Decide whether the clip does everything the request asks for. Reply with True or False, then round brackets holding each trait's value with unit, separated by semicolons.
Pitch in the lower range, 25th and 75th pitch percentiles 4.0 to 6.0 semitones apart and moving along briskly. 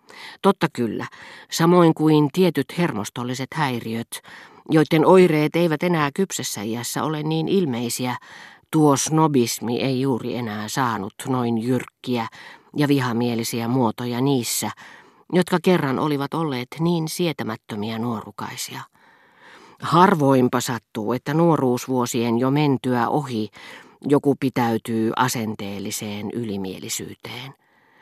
False (130 Hz; 4.9 semitones; 100 wpm)